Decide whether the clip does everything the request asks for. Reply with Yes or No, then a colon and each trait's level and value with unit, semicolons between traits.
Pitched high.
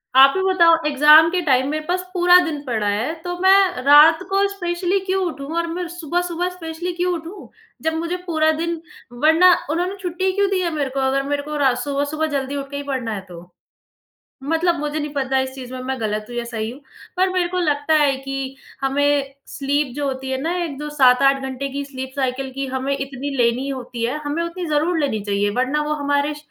Yes: very high, 290 Hz